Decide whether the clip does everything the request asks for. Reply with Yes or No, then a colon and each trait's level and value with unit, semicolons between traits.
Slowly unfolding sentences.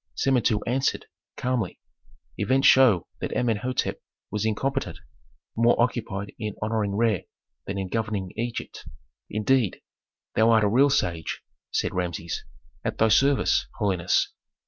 Yes: slow, 125 wpm